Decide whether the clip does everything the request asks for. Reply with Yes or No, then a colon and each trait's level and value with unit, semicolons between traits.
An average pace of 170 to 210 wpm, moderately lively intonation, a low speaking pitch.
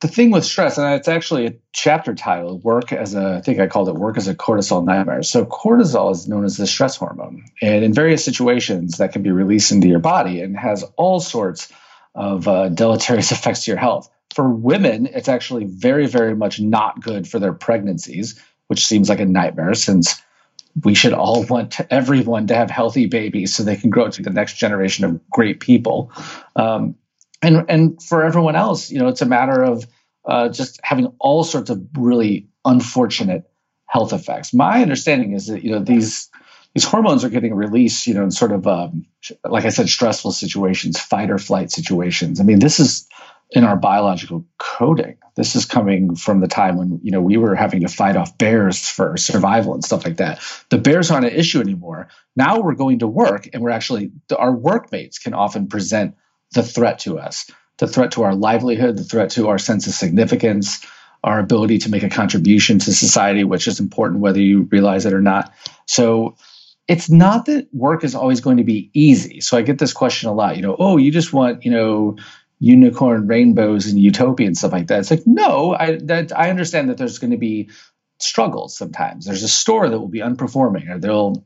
No: fast, 205 wpm; wide, 8.1 semitones; low, 115 Hz